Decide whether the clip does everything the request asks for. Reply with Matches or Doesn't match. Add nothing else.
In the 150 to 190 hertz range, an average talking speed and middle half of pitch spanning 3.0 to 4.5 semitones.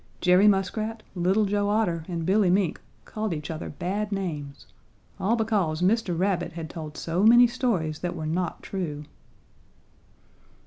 Matches